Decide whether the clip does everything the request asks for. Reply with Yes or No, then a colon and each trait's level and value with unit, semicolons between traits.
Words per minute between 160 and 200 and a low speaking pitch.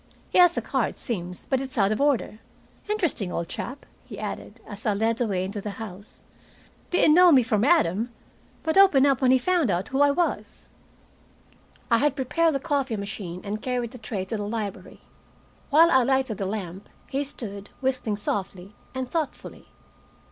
No: average, 185 wpm; high, 240 Hz